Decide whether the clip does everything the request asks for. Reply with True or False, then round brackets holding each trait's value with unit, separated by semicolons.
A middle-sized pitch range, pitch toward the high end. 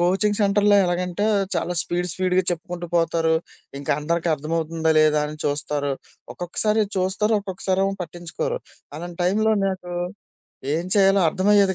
False (3.0 semitones; 175 Hz)